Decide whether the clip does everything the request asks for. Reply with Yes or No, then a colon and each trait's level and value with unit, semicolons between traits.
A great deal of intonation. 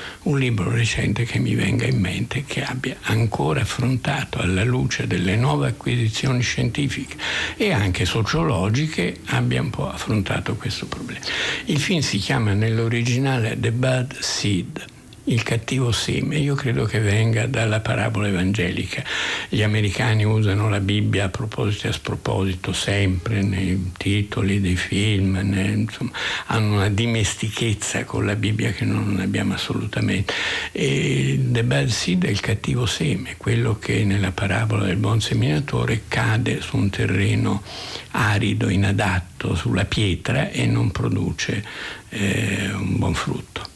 No: average, 3.5 semitones